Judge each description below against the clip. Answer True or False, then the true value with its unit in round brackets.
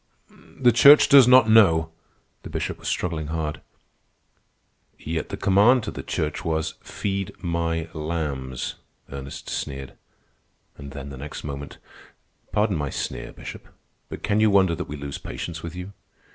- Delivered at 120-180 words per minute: True (150 wpm)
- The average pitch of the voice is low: True (80 Hz)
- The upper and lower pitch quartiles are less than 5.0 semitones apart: False (5.3 semitones)